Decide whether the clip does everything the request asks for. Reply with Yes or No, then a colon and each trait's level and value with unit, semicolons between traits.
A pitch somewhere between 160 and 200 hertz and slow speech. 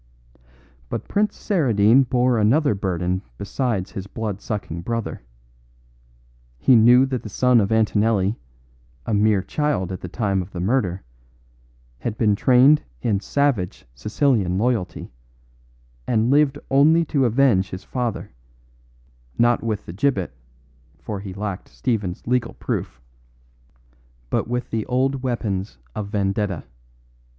No: low, 110 Hz; slow, 125 wpm